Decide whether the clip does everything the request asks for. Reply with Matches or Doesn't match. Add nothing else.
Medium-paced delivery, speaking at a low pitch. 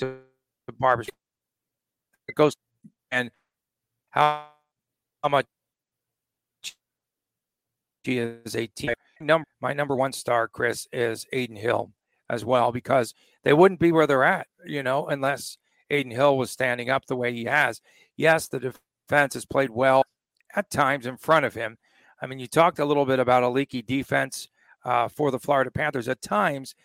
Matches